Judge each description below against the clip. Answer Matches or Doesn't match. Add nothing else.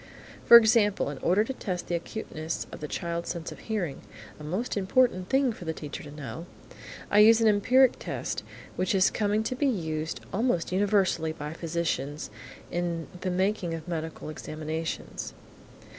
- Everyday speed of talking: Matches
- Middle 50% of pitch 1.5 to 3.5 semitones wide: Doesn't match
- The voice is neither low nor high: Matches